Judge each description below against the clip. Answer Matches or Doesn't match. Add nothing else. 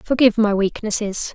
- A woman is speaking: Matches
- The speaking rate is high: Doesn't match